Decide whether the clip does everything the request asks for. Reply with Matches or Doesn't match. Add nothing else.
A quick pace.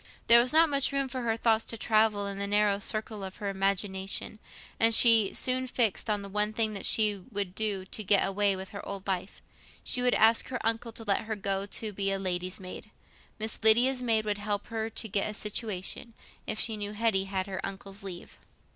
Matches